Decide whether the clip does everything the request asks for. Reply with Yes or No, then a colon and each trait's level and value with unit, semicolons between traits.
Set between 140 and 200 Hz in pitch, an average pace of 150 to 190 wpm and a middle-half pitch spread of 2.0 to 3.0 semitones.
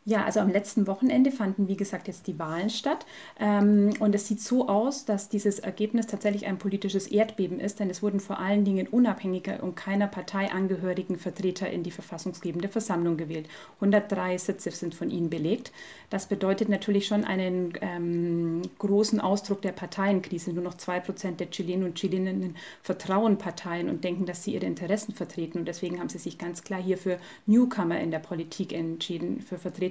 Yes: high, 190 Hz; average, 185 wpm; narrow, 2.4 semitones